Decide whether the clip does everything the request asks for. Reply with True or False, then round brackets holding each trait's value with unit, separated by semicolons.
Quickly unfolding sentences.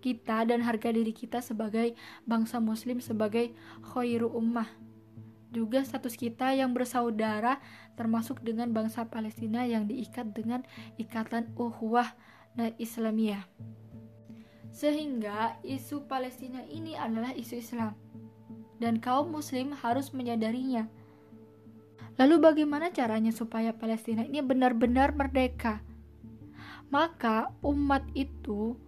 False (105 wpm)